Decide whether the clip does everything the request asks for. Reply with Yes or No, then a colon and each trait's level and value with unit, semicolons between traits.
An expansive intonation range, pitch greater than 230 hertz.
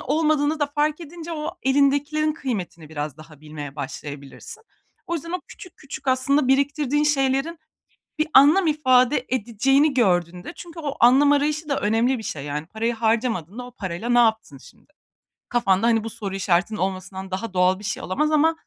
Yes: wide, 7.7 semitones; very high, 250 Hz